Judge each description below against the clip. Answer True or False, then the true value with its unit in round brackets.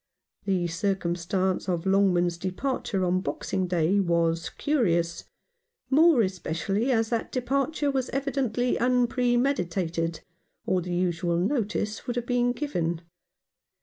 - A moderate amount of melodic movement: False (6.0 semitones)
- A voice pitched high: True (195 Hz)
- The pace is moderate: False (115 wpm)